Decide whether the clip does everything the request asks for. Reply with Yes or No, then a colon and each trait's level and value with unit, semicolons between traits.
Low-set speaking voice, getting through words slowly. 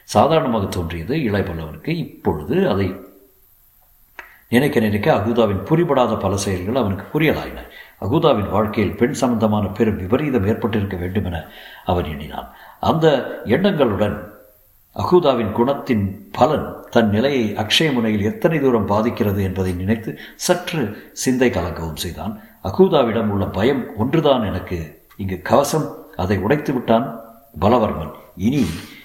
No: low, 105 Hz; average, 110 wpm